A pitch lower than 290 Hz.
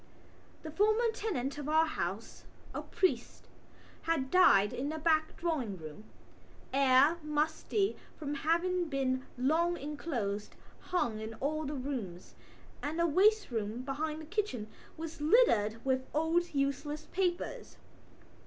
No: very high, 300 Hz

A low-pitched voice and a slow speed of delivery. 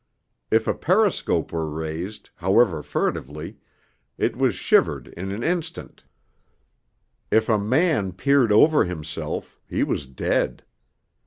Yes: low, 100 Hz; slow, 115 wpm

